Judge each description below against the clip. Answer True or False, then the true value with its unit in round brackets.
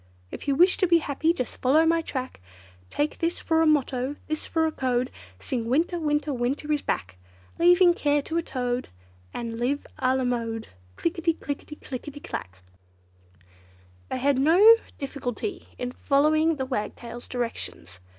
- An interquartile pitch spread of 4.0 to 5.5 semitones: True (4.4 semitones)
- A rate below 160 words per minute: False (170 wpm)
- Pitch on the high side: True (285 Hz)